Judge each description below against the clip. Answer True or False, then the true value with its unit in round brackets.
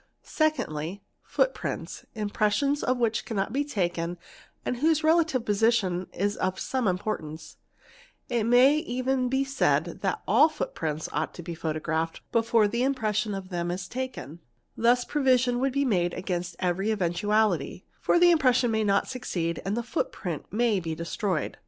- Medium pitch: False (215 Hz)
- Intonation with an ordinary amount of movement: False (6.2 semitones)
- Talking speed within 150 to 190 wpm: True (160 wpm)